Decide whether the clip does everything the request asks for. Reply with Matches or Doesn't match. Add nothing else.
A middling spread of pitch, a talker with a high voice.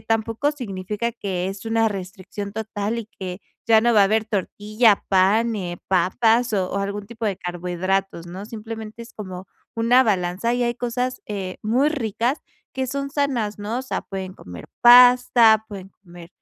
Matches